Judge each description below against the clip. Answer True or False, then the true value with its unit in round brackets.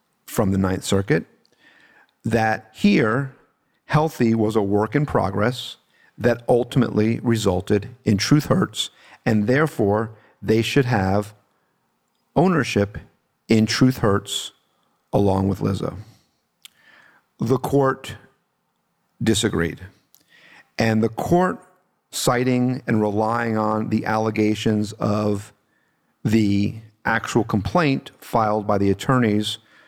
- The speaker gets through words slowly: True (100 wpm)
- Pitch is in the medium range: False (110 Hz)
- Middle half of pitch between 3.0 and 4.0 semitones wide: True (3.3 semitones)